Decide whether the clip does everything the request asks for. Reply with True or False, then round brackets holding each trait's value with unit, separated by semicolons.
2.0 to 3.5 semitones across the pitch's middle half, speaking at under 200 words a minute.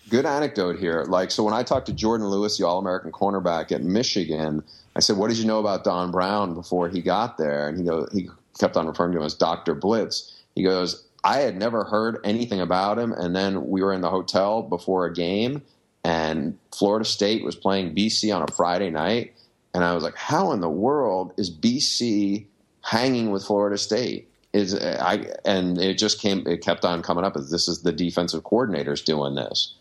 False (3.2 semitones; 205 wpm)